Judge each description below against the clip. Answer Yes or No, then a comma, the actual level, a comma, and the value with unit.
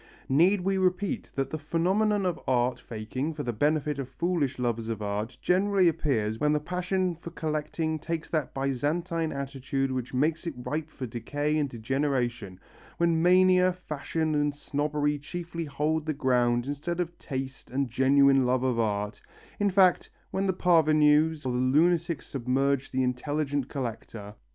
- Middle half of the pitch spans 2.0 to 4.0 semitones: No, average, 4.4 semitones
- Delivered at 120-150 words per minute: No, average, 160 wpm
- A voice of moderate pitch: Yes, medium, 145 Hz